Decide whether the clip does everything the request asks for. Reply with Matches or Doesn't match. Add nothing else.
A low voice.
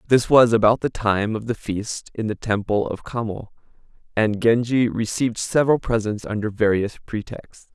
Matches